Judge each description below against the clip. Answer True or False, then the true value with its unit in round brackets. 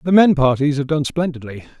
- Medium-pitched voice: True (145 Hz)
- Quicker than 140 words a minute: True (200 wpm)